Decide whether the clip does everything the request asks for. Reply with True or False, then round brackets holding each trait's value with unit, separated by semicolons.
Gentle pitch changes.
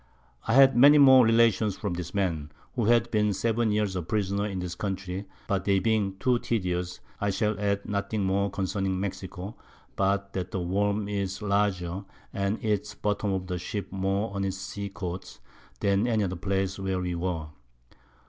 True (2.0 semitones)